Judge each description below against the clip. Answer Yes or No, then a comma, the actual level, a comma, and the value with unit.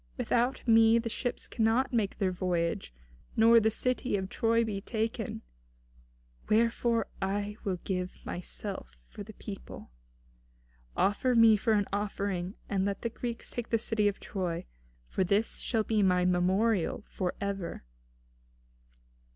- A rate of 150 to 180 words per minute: No, average, 140 wpm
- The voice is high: Yes, high, 205 Hz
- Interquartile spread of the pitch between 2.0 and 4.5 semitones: Yes, average, 3.3 semitones